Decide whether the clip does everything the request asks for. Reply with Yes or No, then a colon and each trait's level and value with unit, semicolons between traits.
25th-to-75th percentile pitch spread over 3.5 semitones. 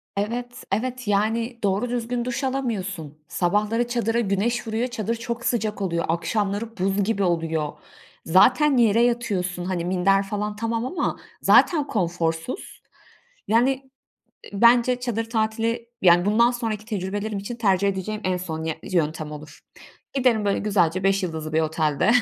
Yes: average, 4.3 semitones